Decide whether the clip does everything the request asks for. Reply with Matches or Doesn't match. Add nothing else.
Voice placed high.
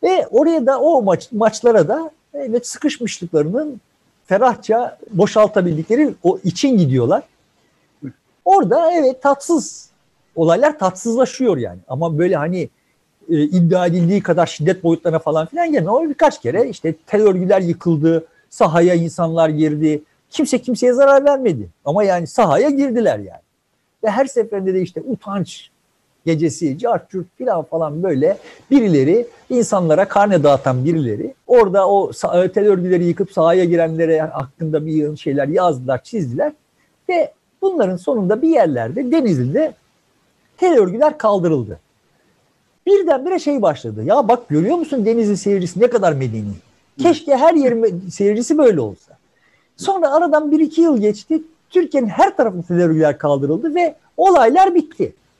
Matches